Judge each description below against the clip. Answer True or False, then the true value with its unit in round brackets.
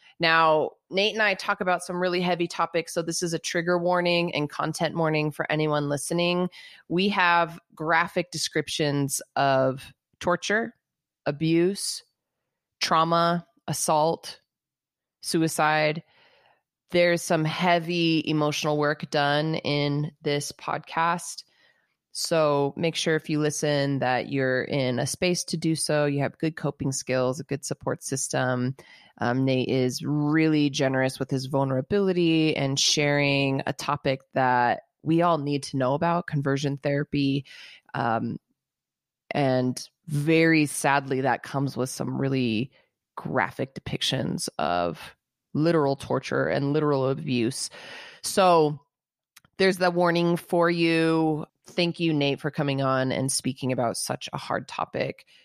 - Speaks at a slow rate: True (130 wpm)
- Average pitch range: True (3.6 semitones)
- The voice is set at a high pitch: False (150 Hz)